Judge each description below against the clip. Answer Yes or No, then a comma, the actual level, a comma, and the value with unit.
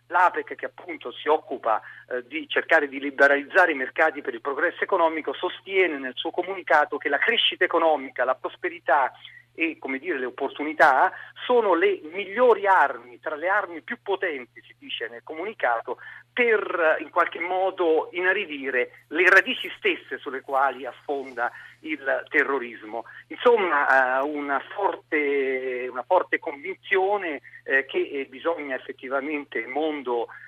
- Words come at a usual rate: Yes, average, 135 wpm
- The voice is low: No, medium, 160 Hz